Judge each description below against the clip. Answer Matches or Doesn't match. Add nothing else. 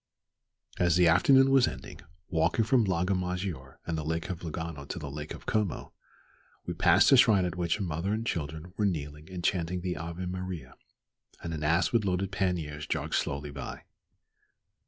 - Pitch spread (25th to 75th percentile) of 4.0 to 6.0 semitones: Doesn't match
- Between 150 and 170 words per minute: Doesn't match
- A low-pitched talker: Matches